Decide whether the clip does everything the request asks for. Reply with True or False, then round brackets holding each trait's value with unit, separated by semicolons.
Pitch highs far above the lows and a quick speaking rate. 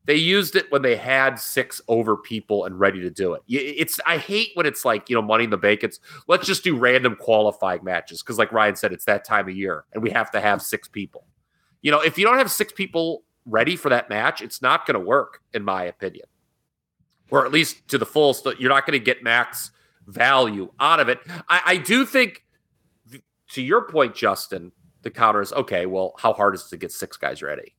True (8.7 semitones; 225 wpm)